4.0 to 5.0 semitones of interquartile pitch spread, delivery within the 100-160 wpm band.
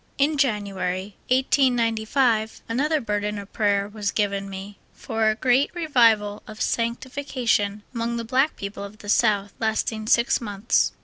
No: average, 3.1 semitones; average, 140 wpm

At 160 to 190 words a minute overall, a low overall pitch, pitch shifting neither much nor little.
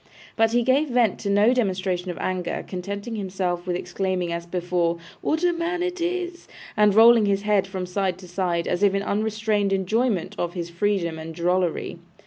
No: average, 185 wpm; high, 195 Hz; average, 3.9 semitones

